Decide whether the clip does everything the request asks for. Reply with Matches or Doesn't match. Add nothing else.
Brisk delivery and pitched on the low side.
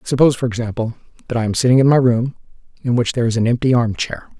Matches